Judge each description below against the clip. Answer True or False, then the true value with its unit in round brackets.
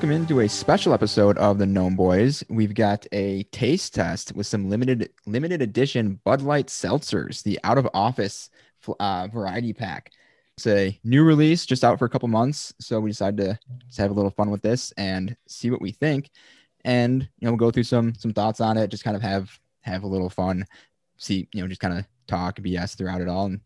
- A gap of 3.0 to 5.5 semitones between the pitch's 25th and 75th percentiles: True (4.2 semitones)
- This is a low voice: True (110 Hz)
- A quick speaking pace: True (220 wpm)